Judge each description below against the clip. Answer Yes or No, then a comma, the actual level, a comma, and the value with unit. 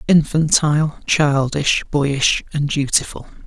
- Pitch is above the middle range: No, medium, 145 Hz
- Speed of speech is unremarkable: No, slow, 85 wpm